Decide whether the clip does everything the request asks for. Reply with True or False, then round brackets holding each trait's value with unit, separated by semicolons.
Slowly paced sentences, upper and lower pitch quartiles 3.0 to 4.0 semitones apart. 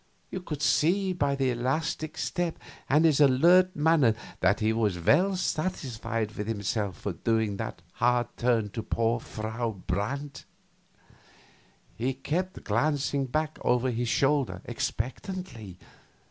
False (130 wpm; 5.6 semitones)